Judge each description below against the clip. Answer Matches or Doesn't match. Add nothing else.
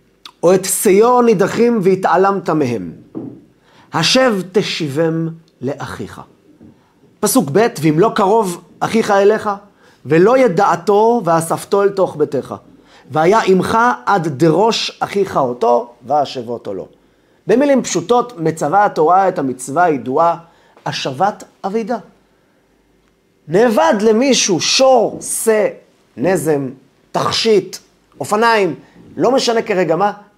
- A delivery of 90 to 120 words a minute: Matches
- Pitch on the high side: Matches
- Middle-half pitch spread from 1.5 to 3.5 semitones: Doesn't match